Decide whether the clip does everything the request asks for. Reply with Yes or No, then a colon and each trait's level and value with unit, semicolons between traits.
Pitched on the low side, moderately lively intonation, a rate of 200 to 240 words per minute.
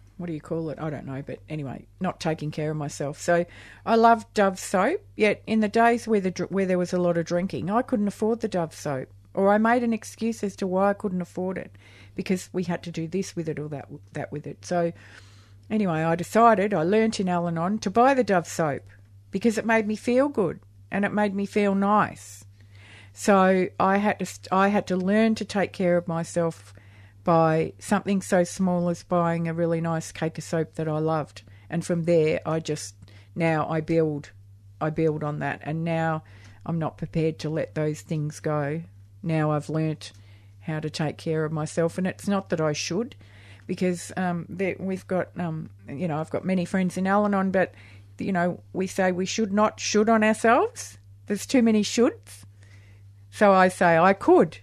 No: medium, 170 Hz; average, 4.7 semitones; fast, 205 wpm